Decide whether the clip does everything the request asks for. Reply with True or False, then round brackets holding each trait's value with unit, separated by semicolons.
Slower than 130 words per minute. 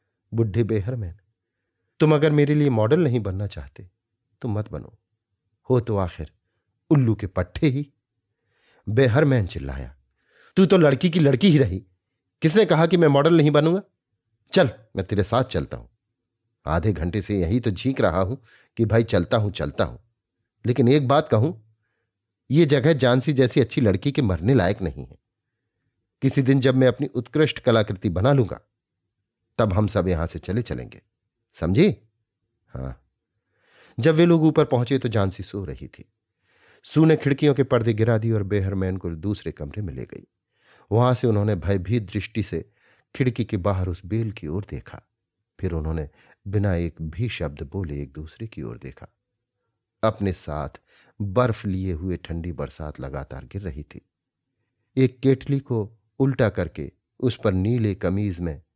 False (165 wpm)